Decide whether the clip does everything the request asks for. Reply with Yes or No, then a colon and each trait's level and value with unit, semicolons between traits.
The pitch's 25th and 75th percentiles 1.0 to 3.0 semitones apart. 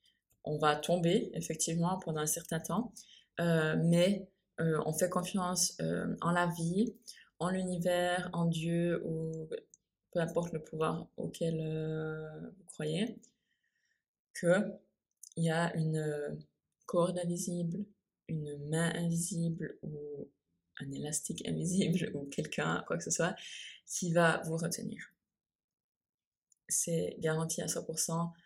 Yes: narrow, 2.4 semitones